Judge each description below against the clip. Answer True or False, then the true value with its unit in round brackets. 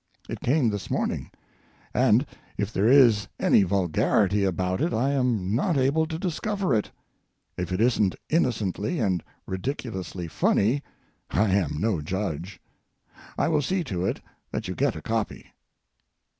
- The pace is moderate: True (145 wpm)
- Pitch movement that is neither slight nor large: False (6.6 semitones)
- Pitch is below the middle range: True (110 Hz)